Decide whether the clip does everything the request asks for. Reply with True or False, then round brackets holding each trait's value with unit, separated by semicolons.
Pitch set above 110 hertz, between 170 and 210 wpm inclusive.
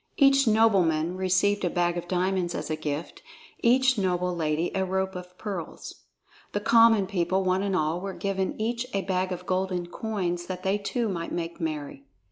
True (185 Hz; 180 wpm)